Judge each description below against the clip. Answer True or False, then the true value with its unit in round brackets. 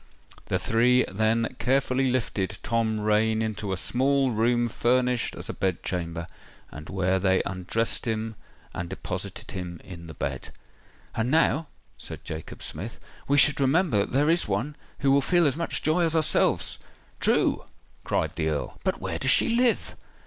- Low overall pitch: True (115 Hz)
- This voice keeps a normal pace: True (165 wpm)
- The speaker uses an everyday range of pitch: False (6.2 semitones)